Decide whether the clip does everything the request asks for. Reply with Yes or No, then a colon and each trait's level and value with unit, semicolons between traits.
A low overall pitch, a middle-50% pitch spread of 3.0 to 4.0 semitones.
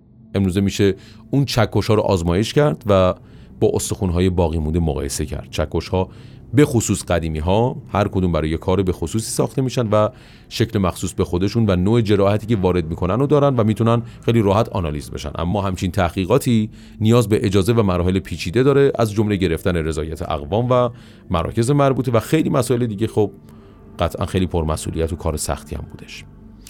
No: low, 100 Hz; average, 4.6 semitones